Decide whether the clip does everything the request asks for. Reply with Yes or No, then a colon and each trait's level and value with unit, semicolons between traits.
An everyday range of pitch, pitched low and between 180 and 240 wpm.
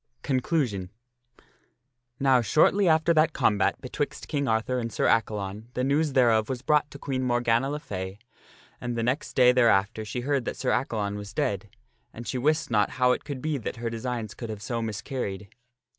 Yes: average, 3.8 semitones; low, 120 Hz; average, 185 wpm